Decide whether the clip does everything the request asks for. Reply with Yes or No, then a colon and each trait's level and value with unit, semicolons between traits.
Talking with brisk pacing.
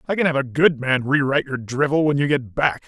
Yes: fast, 270 wpm